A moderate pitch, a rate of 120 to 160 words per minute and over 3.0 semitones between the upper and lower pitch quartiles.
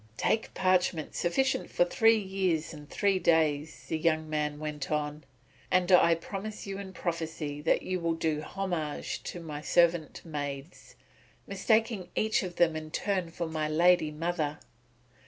Yes: medium, 165 Hz; average, 155 wpm; average, 3.4 semitones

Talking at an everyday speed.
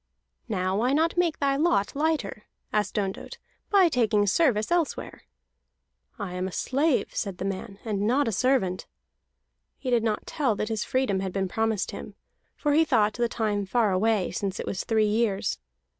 Yes: average, 175 wpm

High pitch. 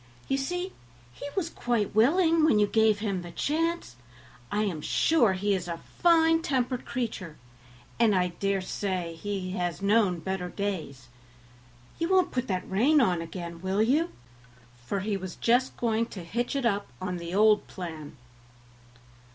Yes: high, 205 Hz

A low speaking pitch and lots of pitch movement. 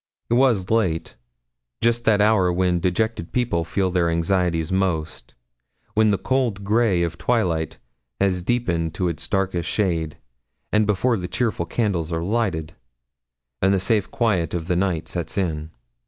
No: very low, 95 Hz; average, 4.3 semitones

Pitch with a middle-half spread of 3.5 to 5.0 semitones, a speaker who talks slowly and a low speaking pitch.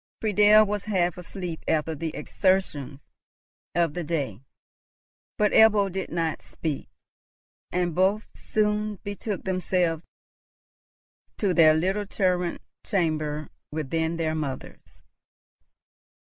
No: average, 4.1 semitones; slow, 105 wpm; medium, 175 Hz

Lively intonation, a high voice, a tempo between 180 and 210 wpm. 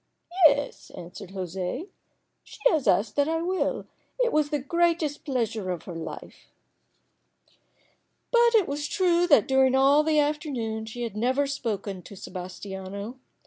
No: wide, 7.1 semitones; very high, 265 Hz; average, 150 wpm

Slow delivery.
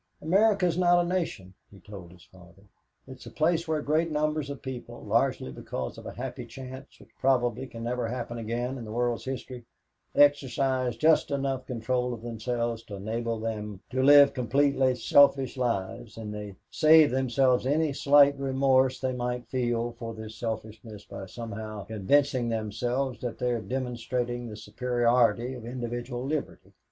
No: average, 165 wpm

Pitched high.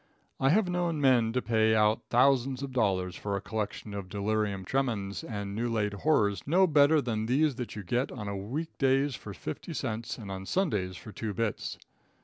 No: low, 115 Hz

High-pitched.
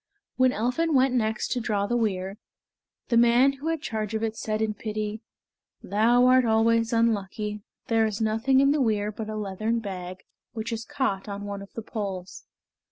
Yes: high, 220 Hz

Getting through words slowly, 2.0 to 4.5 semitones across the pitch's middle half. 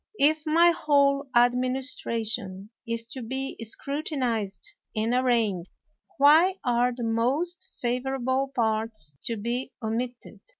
Yes: slow, 110 wpm; average, 3.5 semitones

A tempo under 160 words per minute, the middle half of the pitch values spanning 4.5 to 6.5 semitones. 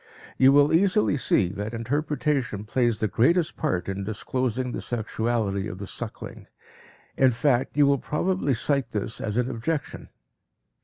Yes: average, 150 wpm; average, 5.0 semitones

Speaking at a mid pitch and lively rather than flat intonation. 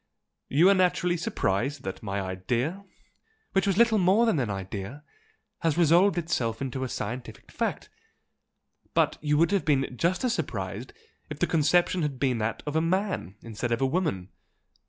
Yes: medium, 150 Hz; wide, 7.3 semitones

